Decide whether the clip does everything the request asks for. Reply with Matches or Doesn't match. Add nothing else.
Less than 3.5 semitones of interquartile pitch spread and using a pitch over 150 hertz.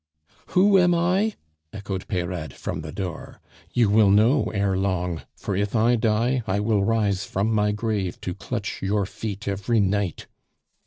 Doesn't match